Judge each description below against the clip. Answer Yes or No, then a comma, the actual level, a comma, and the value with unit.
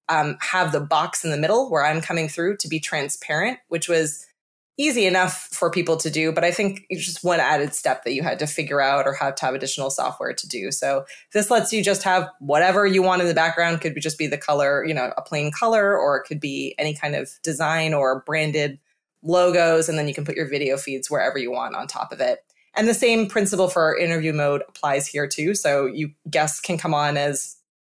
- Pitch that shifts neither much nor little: Yes, average, 3.9 semitones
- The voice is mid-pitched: Yes, medium, 160 Hz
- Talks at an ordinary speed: No, fast, 235 wpm